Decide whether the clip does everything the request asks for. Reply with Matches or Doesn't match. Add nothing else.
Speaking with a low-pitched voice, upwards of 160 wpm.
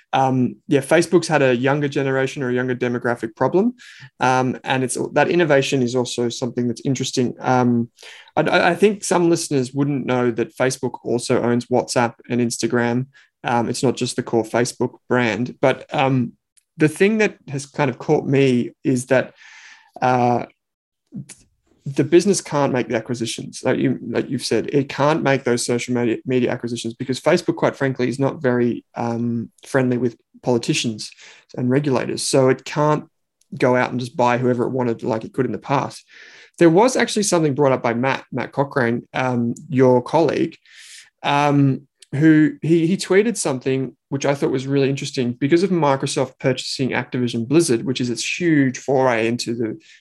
Matches